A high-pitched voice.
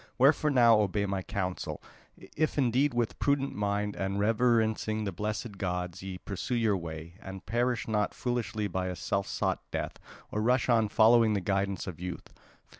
No: low, 105 Hz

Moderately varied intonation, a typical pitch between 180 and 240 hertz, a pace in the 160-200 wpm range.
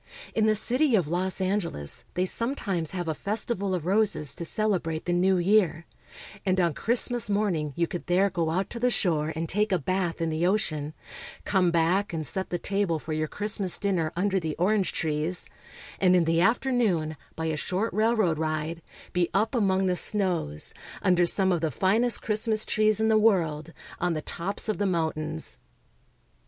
Yes: average, 4.2 semitones; medium, 185 Hz; average, 185 wpm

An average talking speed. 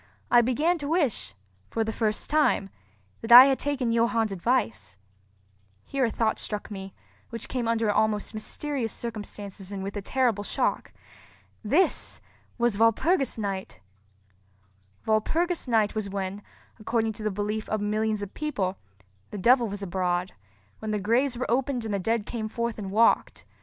Yes: average, 155 wpm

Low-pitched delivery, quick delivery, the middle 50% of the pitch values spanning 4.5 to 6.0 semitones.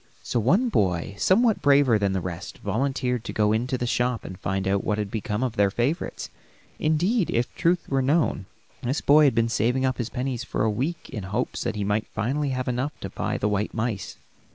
Yes: low, 120 Hz; fast, 220 wpm; average, 4.8 semitones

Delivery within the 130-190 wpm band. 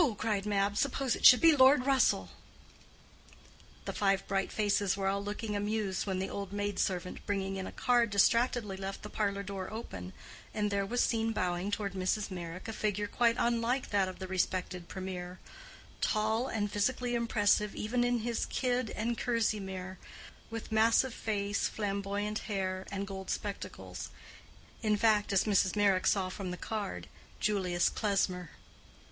Yes: average, 155 wpm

